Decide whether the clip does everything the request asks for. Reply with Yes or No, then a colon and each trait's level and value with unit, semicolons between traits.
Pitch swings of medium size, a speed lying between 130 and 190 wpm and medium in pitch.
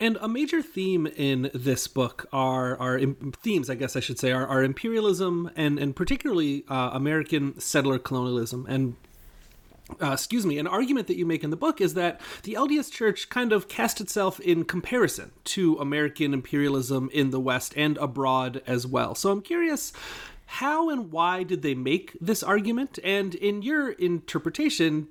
No: wide, 7.3 semitones; average, 175 wpm; medium, 155 Hz